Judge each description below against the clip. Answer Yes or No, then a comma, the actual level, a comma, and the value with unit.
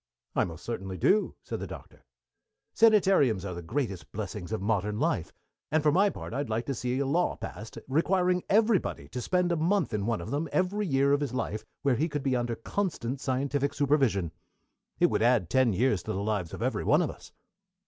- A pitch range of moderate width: No, wide, 6.9 semitones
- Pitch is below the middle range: Yes, low, 130 Hz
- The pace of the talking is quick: Yes, fast, 210 wpm